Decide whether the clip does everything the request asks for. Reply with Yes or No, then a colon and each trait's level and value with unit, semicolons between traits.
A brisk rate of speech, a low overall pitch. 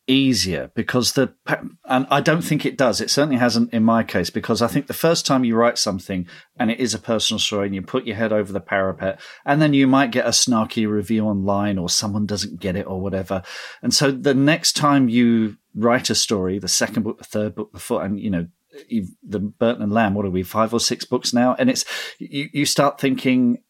Yes: fast, 235 wpm; low, 115 Hz